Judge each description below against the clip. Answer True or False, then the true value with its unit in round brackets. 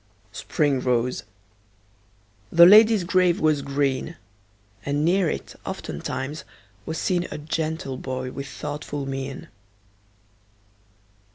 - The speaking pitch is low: False (145 Hz)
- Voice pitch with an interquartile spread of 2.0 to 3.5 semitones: False (4.0 semitones)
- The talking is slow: True (100 wpm)